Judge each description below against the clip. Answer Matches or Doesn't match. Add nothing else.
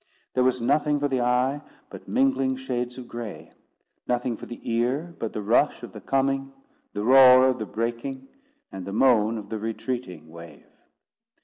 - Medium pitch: Doesn't match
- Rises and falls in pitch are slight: Doesn't match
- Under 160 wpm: Doesn't match